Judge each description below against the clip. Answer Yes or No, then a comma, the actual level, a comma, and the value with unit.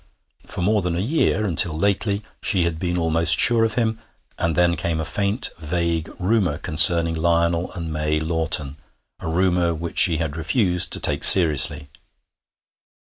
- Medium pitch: No, very low, 85 Hz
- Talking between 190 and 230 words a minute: No, average, 160 wpm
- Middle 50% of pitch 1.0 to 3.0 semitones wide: Yes, average, 2.7 semitones